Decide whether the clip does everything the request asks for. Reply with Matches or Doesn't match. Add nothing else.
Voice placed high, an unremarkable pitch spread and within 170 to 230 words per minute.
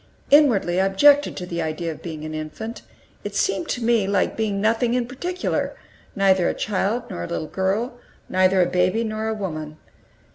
Matches